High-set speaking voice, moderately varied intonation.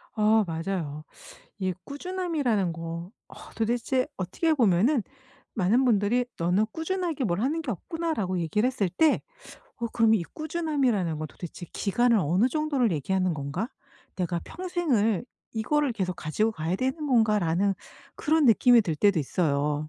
No: high, 215 Hz; wide, 7.1 semitones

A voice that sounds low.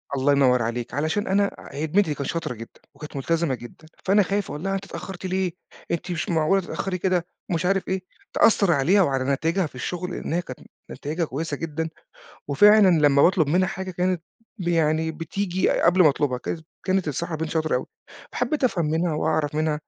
No: medium, 165 Hz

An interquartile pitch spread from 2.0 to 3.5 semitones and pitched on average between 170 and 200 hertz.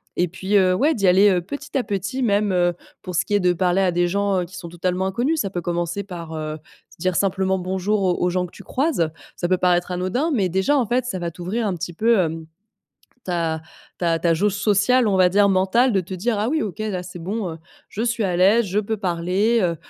Yes: average, 2.9 semitones; high, 190 Hz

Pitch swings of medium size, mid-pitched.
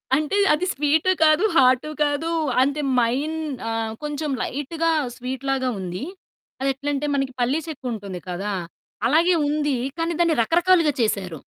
No: average, 4.2 semitones; very high, 285 Hz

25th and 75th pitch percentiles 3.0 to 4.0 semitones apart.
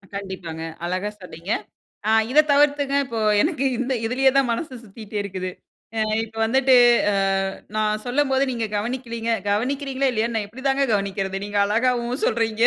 No: average, 4.4 semitones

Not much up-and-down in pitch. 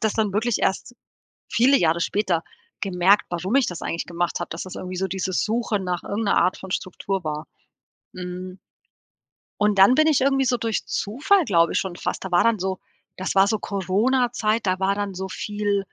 No: average, 3.3 semitones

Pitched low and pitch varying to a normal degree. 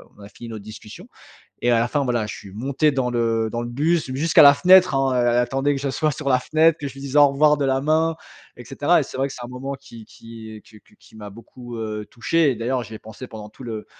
Yes: low, 125 Hz; average, 3.7 semitones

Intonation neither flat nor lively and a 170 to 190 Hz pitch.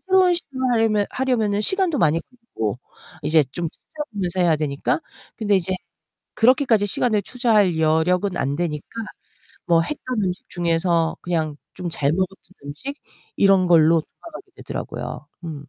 No: wide, 6.3 semitones; medium, 185 Hz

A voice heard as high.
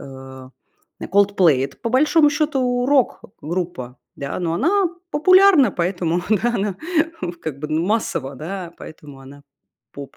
No: medium, 180 Hz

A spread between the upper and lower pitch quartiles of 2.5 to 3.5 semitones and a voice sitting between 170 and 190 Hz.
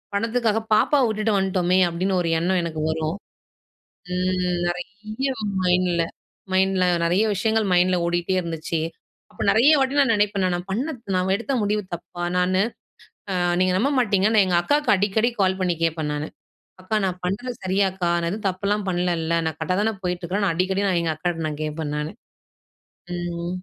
Yes: average, 3.0 semitones; medium, 185 Hz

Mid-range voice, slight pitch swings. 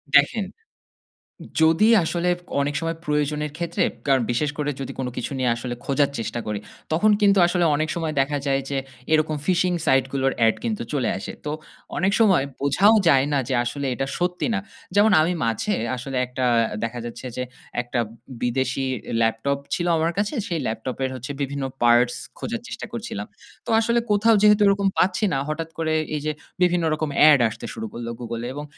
No: medium, 145 Hz; average, 5.3 semitones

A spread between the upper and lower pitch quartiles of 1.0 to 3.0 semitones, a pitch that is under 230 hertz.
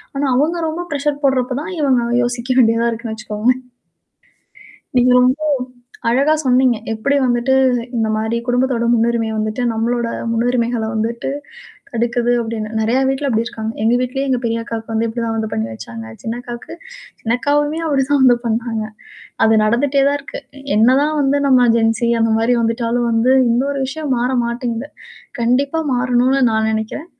No: average, 2.7 semitones; high, 240 Hz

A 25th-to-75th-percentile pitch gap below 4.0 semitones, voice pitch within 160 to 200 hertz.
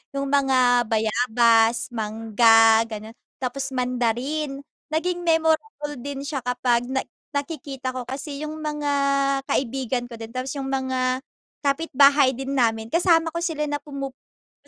No: average, 3.2 semitones; very high, 265 Hz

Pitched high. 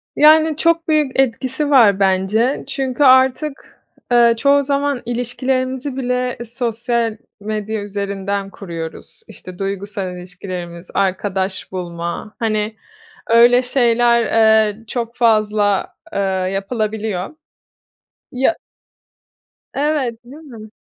Yes: high, 230 Hz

